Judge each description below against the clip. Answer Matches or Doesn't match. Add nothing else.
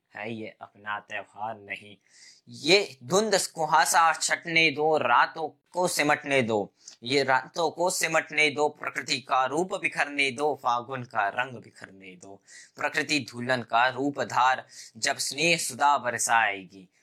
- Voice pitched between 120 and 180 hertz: Matches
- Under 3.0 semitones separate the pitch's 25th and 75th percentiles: Doesn't match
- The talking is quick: Doesn't match